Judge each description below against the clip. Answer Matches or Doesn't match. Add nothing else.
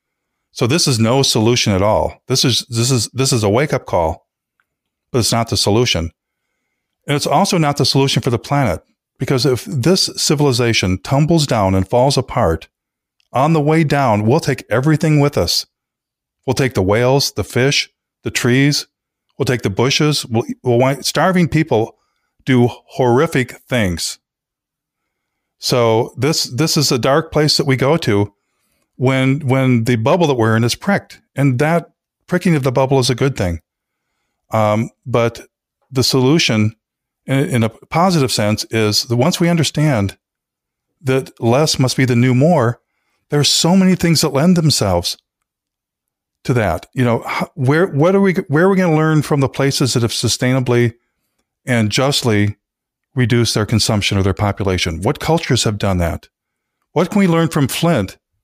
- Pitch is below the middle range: Matches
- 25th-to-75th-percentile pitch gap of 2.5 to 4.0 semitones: Doesn't match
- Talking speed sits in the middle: Matches